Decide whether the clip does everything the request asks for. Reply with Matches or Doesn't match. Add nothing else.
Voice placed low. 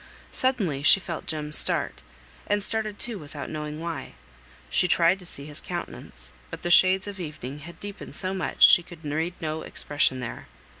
Doesn't match